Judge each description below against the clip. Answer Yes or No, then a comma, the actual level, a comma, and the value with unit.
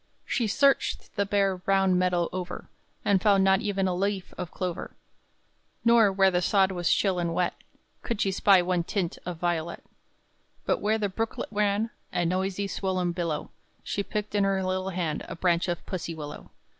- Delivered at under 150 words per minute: No, average, 180 wpm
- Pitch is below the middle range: No, high, 190 Hz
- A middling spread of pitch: No, narrow, 2.2 semitones